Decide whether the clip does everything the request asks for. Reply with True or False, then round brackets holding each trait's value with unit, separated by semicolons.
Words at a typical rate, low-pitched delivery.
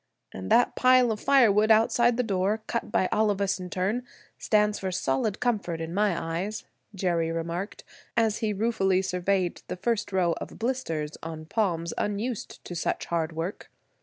False (170 wpm; 195 Hz)